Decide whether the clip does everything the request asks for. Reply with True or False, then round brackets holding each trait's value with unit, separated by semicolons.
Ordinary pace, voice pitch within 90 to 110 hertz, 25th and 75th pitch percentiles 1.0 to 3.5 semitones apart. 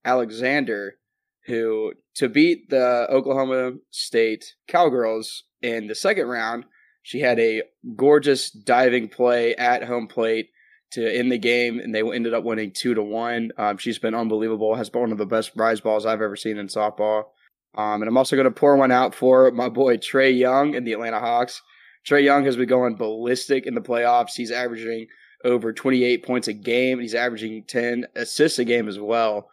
False (190 wpm; 120 Hz; 2.5 semitones)